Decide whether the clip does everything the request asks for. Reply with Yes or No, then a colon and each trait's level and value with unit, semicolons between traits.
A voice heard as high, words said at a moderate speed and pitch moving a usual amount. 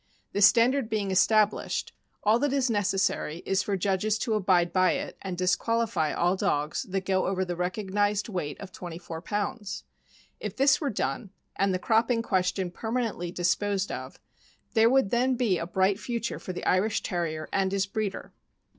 Yes: high, 195 Hz; average, 175 wpm; average, 3.4 semitones